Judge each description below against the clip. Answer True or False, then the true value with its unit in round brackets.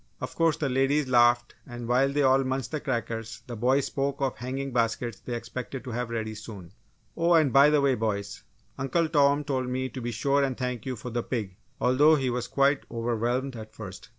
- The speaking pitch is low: True (125 Hz)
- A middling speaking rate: False (215 wpm)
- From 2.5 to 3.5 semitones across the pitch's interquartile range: True (2.8 semitones)